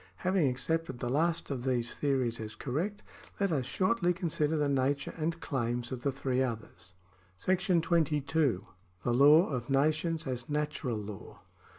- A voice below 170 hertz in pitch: Yes, medium, 140 Hz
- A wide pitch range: No, average, 4.7 semitones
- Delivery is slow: No, average, 155 wpm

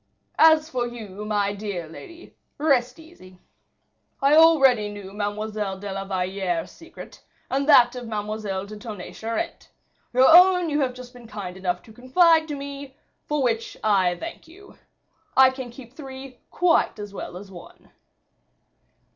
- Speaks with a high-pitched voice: Yes, high, 240 Hz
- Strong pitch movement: Yes, wide, 5.7 semitones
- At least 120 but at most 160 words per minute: Yes, average, 155 wpm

